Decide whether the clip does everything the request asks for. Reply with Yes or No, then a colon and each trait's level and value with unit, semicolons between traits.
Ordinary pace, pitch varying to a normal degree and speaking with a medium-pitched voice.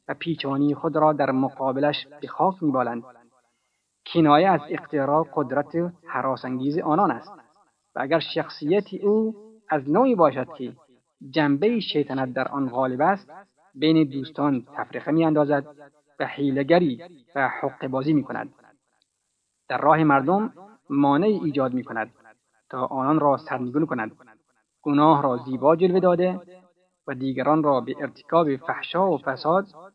Yes: average, 130 wpm; average, 4.1 semitones; medium, 145 Hz